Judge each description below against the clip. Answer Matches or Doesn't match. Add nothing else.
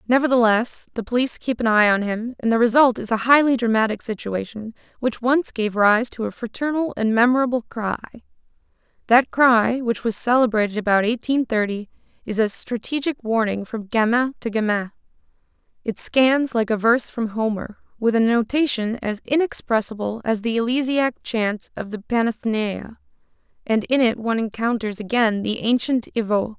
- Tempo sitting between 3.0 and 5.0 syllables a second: Doesn't match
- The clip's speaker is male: Doesn't match